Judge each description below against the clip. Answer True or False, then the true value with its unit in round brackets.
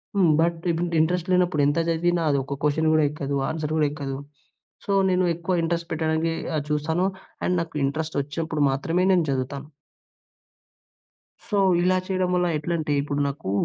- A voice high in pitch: False (160 Hz)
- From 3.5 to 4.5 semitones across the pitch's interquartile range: False (2.9 semitones)